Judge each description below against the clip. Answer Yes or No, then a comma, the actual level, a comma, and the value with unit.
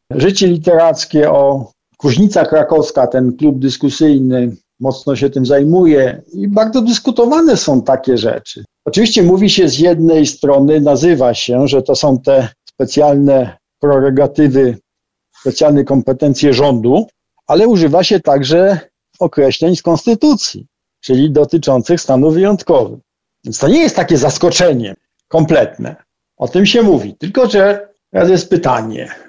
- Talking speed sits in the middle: Yes, average, 125 wpm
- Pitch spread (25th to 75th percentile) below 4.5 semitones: No, average, 5.1 semitones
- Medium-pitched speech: Yes, medium, 150 Hz